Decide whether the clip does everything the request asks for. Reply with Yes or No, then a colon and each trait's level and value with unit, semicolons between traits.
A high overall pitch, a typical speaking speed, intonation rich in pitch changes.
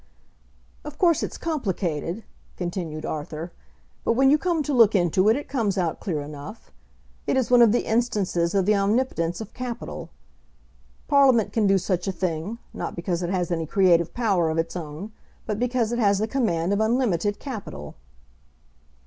Yes: high, 200 Hz; average, 175 wpm; wide, 5.7 semitones